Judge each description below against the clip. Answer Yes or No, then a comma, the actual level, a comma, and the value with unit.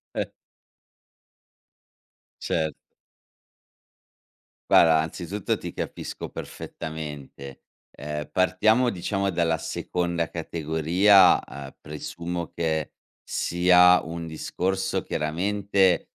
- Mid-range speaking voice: No, very low, 85 Hz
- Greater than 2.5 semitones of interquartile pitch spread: Yes, average, 2.9 semitones